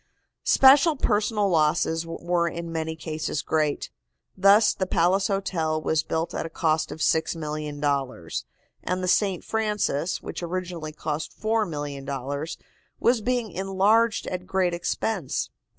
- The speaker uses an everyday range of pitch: Yes, average, 4.1 semitones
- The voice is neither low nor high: Yes, medium, 170 Hz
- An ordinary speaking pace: No, slow, 125 wpm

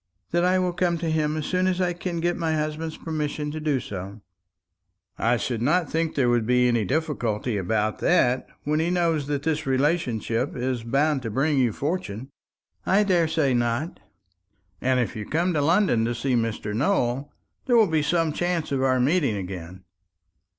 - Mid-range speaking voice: Yes, medium, 145 Hz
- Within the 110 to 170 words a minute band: No, average, 185 wpm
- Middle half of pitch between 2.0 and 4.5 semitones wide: No, wide, 5.5 semitones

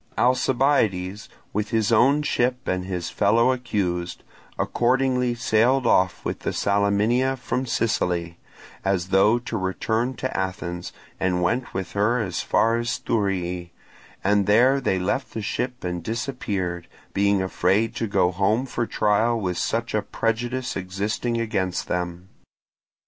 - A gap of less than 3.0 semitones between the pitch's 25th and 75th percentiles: No, average, 4.4 semitones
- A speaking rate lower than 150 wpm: Yes, average, 140 wpm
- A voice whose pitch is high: No, low, 105 Hz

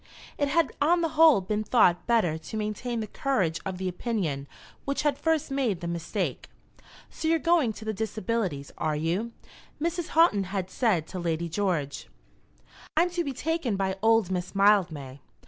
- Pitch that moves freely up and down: Yes, wide, 7.8 semitones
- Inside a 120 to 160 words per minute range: No, average, 170 wpm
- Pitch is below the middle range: No, high, 210 Hz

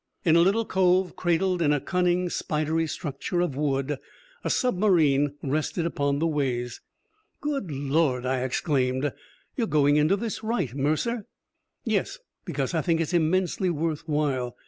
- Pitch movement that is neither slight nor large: Yes, average, 4.2 semitones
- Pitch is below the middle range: No, medium, 155 Hz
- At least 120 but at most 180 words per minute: Yes, average, 145 wpm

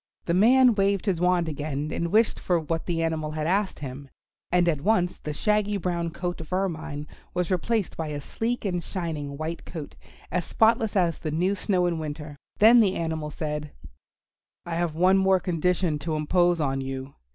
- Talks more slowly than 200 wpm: Yes, average, 185 wpm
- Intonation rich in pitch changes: No, average, 3.7 semitones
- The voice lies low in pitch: No, medium, 170 Hz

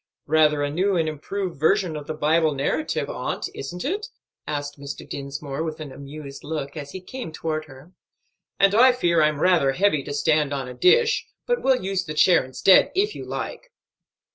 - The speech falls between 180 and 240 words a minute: Yes, average, 190 wpm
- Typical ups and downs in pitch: Yes, average, 5.0 semitones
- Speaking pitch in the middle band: Yes, medium, 155 Hz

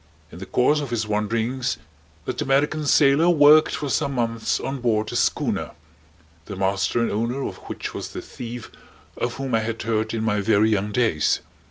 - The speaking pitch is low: Yes, low, 115 Hz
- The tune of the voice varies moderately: Yes, average, 3.9 semitones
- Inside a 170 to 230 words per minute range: Yes, average, 185 wpm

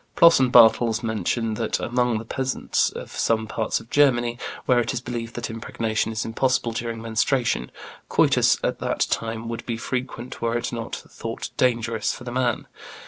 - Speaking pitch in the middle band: No, low, 115 Hz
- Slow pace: No, average, 175 wpm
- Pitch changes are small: Yes, narrow, 1.5 semitones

